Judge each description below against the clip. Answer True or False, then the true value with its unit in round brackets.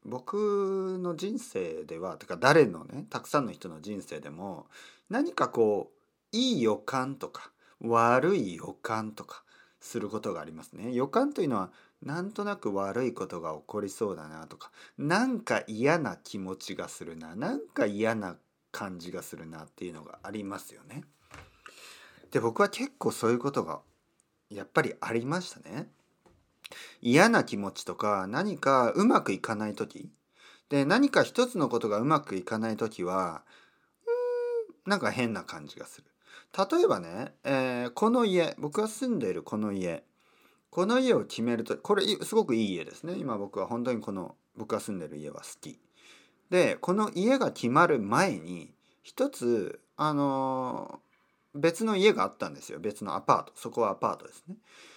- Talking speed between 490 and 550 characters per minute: False (305 characters per minute)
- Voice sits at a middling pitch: True (145 Hz)